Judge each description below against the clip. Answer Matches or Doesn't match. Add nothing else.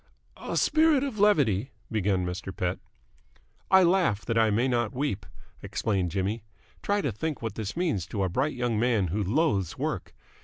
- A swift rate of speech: Doesn't match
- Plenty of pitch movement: Matches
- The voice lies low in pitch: Matches